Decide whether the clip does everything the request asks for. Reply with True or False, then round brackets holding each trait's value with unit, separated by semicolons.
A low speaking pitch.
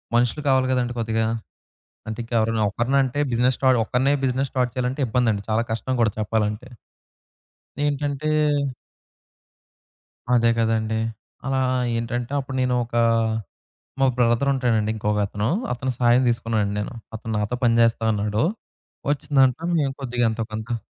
True (120 Hz)